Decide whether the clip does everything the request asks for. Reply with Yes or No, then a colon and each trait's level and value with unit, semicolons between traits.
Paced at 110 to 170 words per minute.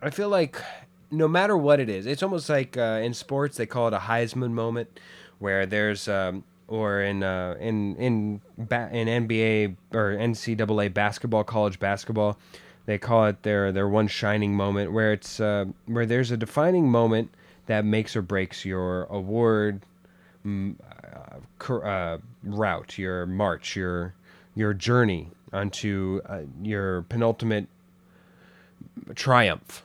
Yes: average, 140 wpm